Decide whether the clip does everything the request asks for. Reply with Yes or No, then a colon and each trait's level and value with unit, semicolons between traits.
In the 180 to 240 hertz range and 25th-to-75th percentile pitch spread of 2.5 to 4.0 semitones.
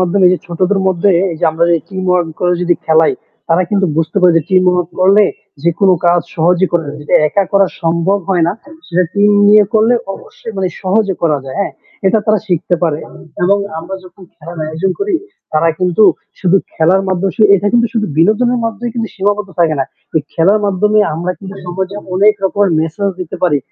Yes: medium, 185 Hz; average, 2.9 semitones